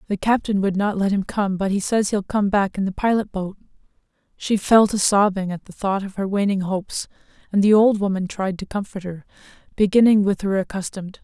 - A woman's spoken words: Yes, female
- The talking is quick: Yes, fast, 215 wpm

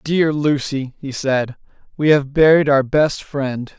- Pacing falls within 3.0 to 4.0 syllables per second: Yes, 3.7 syllables/s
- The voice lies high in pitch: No, medium, 140 Hz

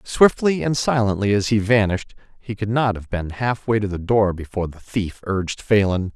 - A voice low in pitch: Yes, low, 105 Hz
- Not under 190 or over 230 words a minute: Yes, fast, 205 wpm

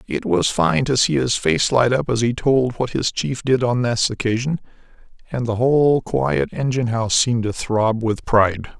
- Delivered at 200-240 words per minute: Yes, fast, 205 wpm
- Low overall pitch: Yes, low, 115 Hz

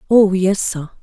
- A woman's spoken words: Yes, female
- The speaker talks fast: No, average, 175 wpm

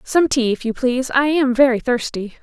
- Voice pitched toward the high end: Yes, very high, 255 Hz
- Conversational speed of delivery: No, fast, 225 wpm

